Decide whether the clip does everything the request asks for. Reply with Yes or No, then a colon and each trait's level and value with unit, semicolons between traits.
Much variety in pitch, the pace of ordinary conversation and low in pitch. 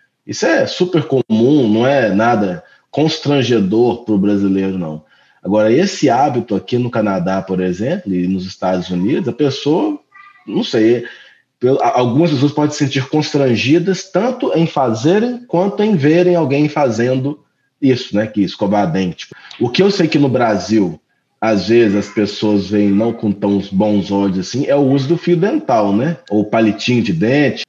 Yes: wide, 7.8 semitones; average, 165 wpm; low, 125 Hz